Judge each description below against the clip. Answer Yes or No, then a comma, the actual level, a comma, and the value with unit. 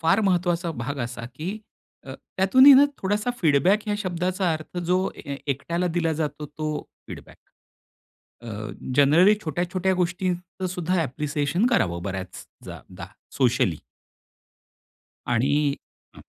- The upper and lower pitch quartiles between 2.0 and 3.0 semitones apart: No, average, 4.7 semitones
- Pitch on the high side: No, medium, 170 Hz